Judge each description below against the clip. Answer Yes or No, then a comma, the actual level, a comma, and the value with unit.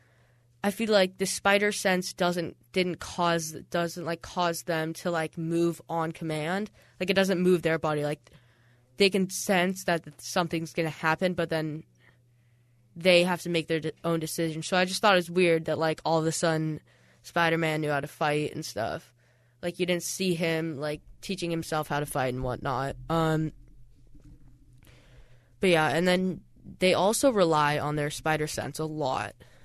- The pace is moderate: Yes, average, 180 wpm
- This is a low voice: No, medium, 160 Hz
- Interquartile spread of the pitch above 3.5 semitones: No, average, 3.2 semitones